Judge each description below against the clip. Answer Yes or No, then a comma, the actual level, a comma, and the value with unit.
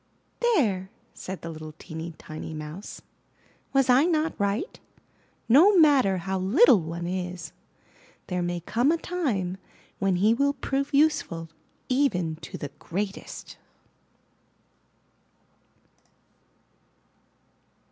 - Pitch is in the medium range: No, high, 195 Hz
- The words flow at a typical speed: No, slow, 105 wpm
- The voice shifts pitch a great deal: Yes, wide, 8.3 semitones